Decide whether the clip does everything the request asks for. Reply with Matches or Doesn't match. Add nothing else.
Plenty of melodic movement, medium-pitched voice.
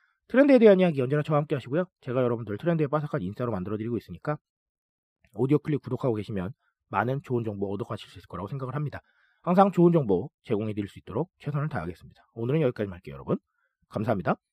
Doesn't match